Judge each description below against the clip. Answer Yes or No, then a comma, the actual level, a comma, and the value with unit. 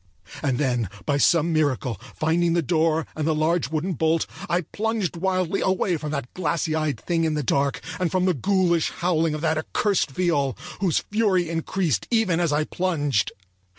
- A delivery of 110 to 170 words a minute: No, average, 180 wpm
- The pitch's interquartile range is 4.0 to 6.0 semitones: No, average, 3.2 semitones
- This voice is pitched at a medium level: Yes, medium, 165 Hz